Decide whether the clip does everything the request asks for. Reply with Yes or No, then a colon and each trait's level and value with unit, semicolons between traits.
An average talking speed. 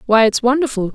Yes: average, 190 wpm